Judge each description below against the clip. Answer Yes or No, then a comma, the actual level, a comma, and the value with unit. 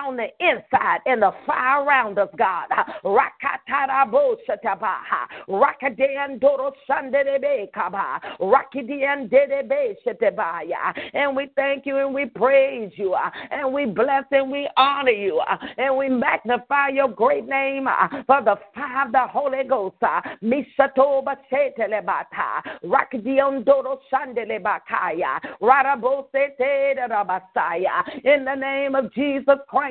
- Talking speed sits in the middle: No, slow, 120 wpm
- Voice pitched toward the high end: Yes, very high, 275 Hz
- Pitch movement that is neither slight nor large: No, narrow, 1.4 semitones